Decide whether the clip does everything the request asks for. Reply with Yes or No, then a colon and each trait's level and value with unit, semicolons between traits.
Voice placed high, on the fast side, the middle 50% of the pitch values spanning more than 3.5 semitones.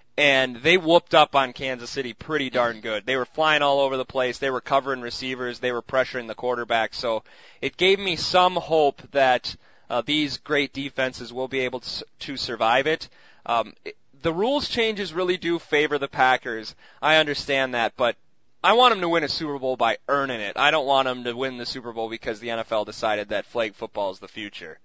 No: low, 135 Hz; fast, 215 wpm; average, 3.9 semitones